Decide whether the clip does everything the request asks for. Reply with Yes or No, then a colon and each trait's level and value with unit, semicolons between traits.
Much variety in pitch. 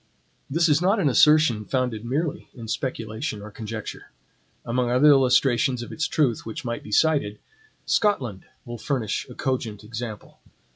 No: average, 4.5 semitones